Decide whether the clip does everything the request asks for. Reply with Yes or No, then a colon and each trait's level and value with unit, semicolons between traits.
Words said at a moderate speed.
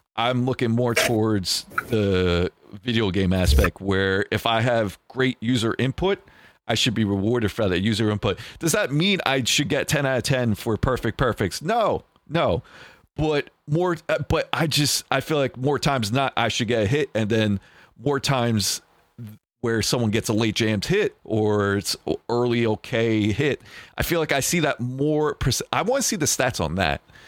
Yes: average, 185 wpm